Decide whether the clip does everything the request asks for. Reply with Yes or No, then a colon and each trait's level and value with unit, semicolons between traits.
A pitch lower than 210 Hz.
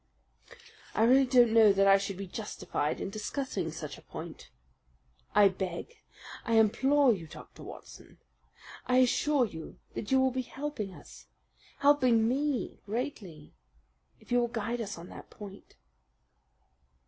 No: high, 230 Hz